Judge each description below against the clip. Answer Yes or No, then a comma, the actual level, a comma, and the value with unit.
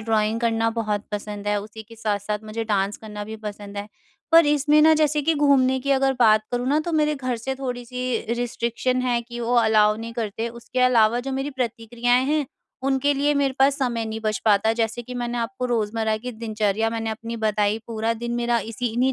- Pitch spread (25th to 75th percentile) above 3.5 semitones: No, average, 2.9 semitones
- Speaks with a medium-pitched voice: No, high, 235 Hz